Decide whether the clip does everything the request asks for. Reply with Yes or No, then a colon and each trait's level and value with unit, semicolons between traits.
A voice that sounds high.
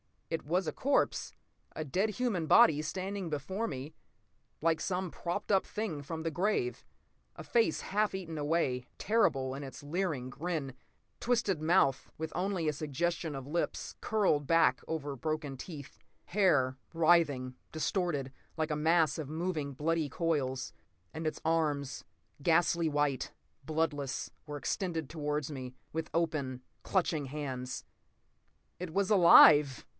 No: medium, 160 Hz